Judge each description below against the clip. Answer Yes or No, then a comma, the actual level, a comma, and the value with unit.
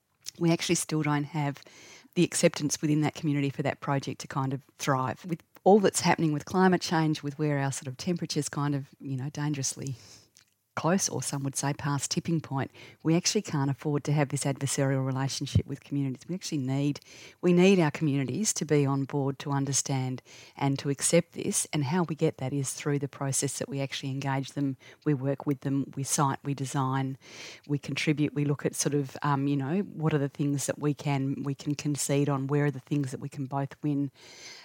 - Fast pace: Yes, fast, 210 wpm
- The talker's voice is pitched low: No, medium, 145 Hz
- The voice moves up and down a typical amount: No, narrow, 2.0 semitones